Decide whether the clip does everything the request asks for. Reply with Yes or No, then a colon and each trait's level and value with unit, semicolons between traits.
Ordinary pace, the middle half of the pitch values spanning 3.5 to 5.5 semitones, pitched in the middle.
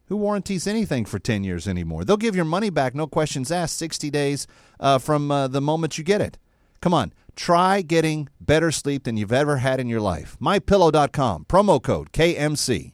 Yes: average, 195 wpm; average, 4.8 semitones; medium, 150 Hz